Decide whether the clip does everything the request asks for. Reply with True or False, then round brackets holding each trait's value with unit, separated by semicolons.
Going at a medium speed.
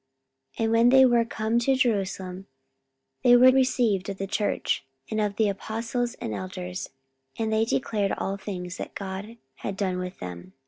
True (175 wpm)